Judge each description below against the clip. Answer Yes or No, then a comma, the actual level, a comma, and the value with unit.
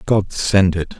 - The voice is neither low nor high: No, very low, 95 Hz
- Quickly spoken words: No, average, 180 wpm